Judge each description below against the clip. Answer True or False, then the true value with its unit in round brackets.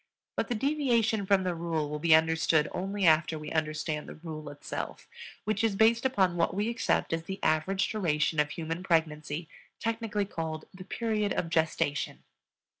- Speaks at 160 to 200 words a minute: True (170 wpm)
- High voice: False (170 Hz)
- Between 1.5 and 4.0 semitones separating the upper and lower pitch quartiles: False (4.7 semitones)